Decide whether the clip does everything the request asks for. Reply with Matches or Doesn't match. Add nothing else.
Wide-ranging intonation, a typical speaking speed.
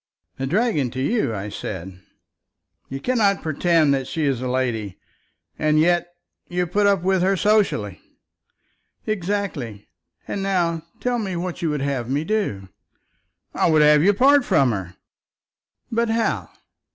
Matches